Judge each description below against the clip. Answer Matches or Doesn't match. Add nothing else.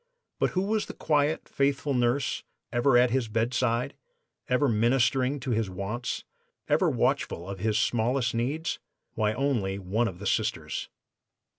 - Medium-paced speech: Matches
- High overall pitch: Doesn't match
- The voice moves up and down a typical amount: Matches